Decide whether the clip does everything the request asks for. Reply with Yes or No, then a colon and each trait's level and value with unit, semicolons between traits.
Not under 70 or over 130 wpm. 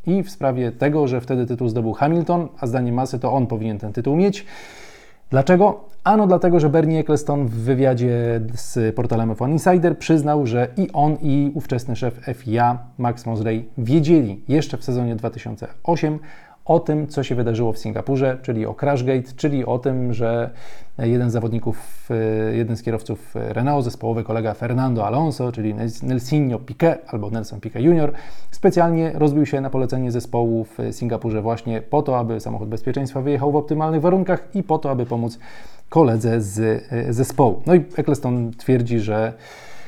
No: fast, 160 wpm